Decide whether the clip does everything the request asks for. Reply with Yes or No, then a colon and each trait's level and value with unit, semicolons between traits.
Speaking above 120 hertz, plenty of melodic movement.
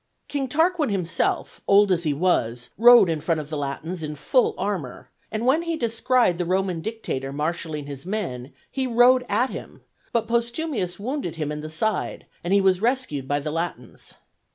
Yes: medium, 185 Hz; wide, 7.5 semitones